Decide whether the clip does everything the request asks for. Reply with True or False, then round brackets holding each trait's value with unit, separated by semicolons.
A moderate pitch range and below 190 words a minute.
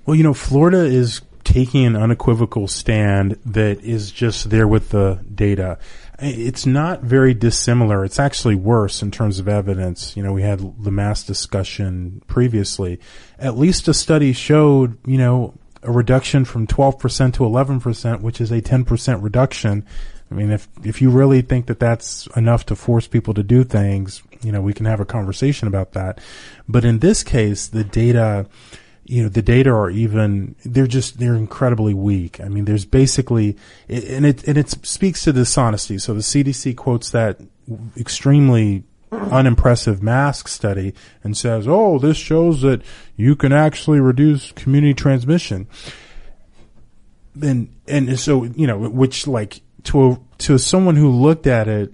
True (4.2 semitones; 165 wpm)